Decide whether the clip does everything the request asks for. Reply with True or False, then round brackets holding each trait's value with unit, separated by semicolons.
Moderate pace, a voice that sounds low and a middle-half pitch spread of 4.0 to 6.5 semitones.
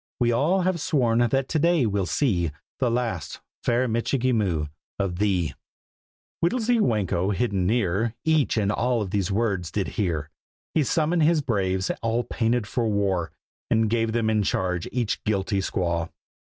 True (160 wpm; 110 Hz; 4.7 semitones)